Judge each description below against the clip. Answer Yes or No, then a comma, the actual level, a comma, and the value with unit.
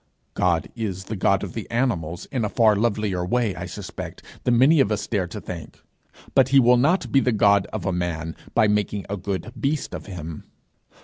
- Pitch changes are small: No, average, 4.8 semitones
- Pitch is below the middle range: Yes, low, 105 Hz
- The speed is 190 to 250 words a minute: Yes, fast, 205 wpm